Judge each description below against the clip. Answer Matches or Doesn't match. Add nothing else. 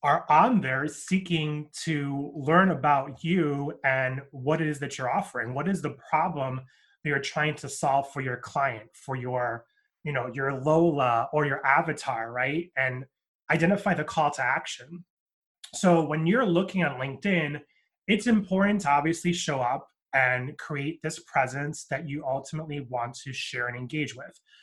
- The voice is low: Doesn't match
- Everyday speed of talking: Matches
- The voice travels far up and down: Doesn't match